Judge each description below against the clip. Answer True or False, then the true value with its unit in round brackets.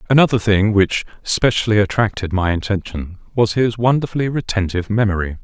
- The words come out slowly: True (130 wpm)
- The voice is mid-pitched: False (105 Hz)